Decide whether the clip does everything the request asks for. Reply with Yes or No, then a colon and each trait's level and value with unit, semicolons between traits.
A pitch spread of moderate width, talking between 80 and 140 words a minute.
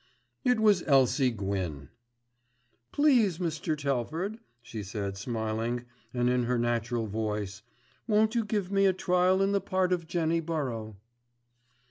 No: wide, 8.9 semitones; slow, 135 wpm